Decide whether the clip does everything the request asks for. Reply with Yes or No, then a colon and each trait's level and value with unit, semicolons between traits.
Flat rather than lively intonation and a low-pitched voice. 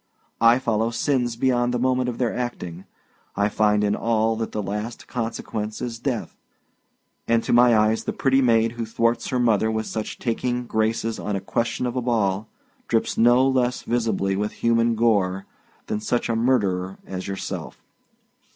Yes: narrow, 2.2 semitones; low, 115 Hz